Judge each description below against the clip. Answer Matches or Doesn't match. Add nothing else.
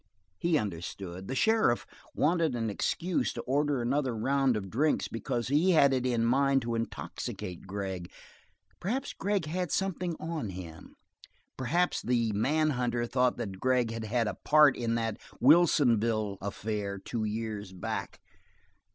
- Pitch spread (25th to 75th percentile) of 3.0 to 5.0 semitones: Doesn't match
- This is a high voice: Doesn't match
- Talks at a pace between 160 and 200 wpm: Doesn't match